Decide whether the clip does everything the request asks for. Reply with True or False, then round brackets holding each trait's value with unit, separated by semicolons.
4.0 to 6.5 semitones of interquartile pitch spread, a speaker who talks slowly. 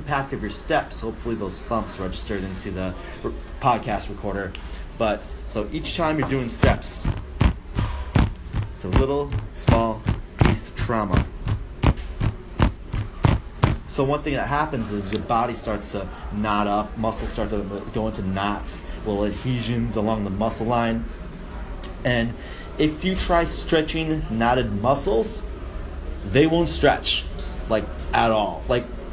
False (3.6 semitones; 130 wpm)